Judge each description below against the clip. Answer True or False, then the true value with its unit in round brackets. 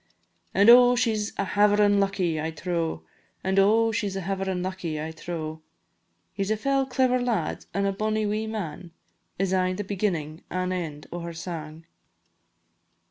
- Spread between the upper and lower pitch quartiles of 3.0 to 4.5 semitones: True (3.9 semitones)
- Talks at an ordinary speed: True (175 wpm)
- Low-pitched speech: False (195 Hz)